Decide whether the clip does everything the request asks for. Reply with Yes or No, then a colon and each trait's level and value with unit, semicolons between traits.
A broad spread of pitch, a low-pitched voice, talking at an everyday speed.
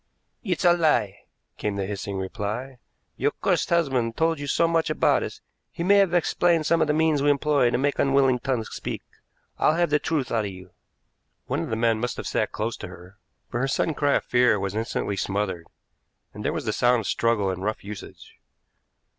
No: wide, 6.8 semitones; low, 125 Hz; fast, 210 wpm